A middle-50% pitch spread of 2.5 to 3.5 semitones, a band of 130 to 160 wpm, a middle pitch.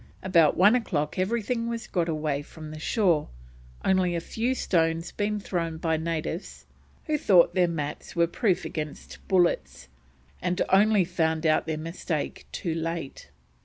Yes: average, 3.2 semitones; average, 150 wpm; medium, 170 Hz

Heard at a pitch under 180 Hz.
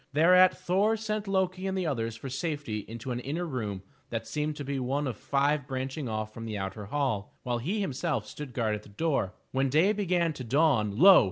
Yes: medium, 140 Hz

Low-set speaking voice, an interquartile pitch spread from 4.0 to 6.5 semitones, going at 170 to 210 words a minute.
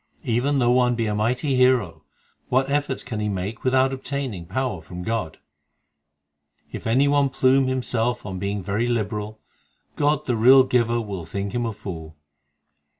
No: low, 120 Hz; average, 4.3 semitones; average, 160 wpm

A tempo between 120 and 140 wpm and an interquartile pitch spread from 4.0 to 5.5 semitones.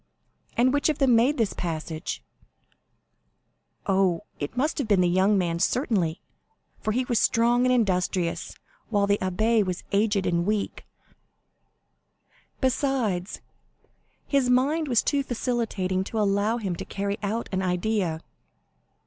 Yes: slow, 135 wpm; average, 4.7 semitones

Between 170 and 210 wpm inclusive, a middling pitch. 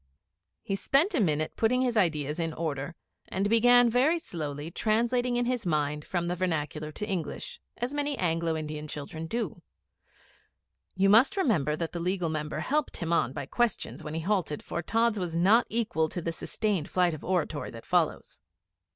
Yes: average, 175 wpm; medium, 180 Hz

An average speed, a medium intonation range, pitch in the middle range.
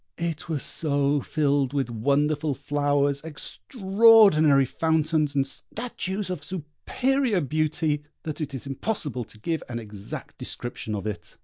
No: slow, 130 wpm; average, 3.2 semitones; medium, 150 Hz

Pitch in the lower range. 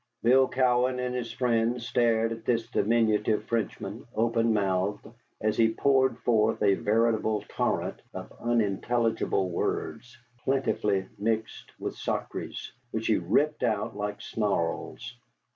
Yes: low, 115 Hz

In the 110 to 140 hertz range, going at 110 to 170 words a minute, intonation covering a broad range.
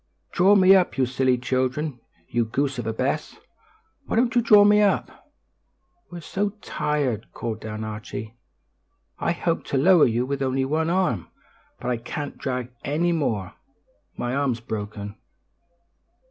Yes: low, 135 Hz; average, 150 wpm; wide, 6.4 semitones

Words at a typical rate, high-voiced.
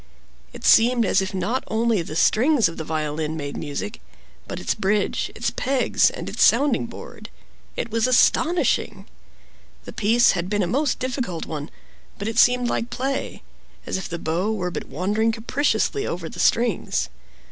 Yes: average, 165 wpm; high, 220 Hz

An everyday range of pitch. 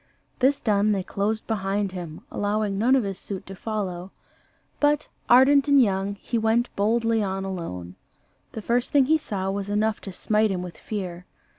Yes: average, 3.0 semitones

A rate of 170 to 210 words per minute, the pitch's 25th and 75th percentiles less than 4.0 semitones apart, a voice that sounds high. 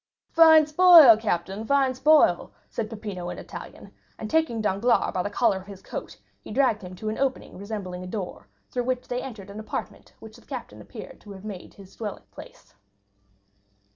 No: average, 185 wpm; average, 5.0 semitones; high, 215 Hz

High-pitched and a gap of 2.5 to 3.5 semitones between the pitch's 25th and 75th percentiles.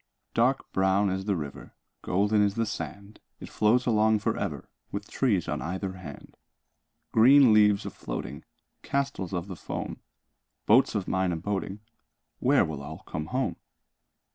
No: low, 100 Hz; average, 2.8 semitones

